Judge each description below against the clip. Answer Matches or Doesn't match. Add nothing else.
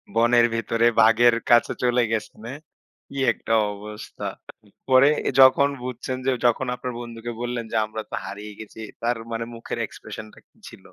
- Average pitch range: Doesn't match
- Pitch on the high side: Doesn't match